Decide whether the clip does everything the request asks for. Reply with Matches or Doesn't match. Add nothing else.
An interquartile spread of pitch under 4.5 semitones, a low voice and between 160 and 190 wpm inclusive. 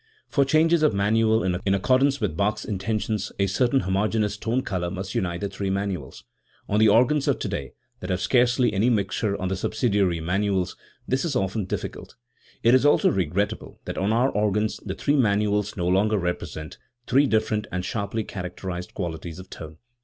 Matches